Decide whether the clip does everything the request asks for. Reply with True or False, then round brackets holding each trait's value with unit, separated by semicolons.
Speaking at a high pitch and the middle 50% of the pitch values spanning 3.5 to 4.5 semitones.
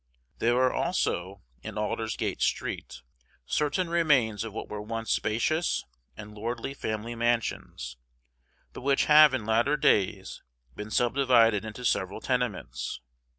False (115 Hz; 3.8 semitones)